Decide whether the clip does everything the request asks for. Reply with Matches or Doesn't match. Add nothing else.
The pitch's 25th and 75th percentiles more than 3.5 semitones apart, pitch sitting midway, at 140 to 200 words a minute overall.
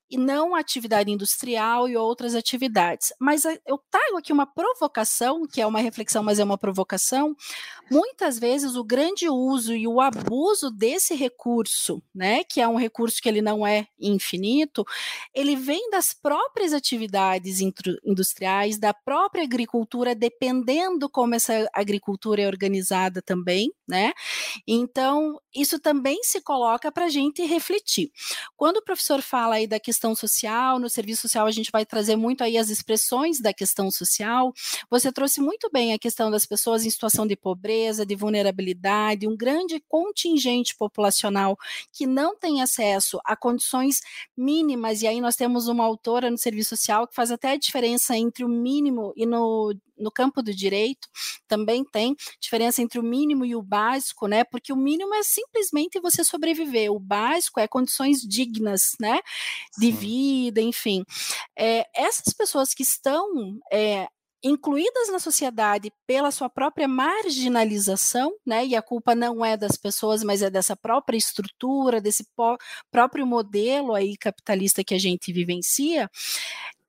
Doesn't match